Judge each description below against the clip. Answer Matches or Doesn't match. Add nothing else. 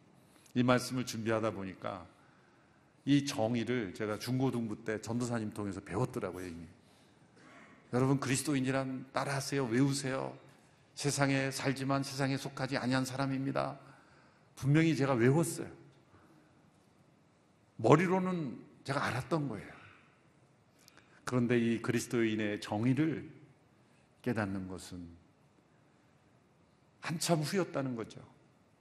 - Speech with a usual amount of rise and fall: Matches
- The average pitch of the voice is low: Matches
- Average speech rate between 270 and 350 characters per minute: Doesn't match